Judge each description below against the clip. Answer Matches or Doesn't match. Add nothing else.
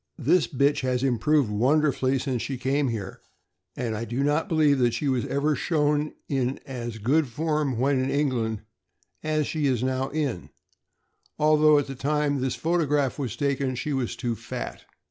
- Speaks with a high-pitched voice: Doesn't match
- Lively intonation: Doesn't match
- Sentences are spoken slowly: Doesn't match